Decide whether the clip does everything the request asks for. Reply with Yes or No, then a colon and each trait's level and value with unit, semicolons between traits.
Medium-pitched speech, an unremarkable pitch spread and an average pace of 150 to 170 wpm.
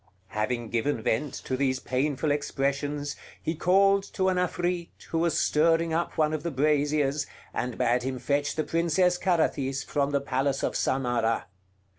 Yes: medium, 145 Hz; average, 3.9 semitones; average, 160 wpm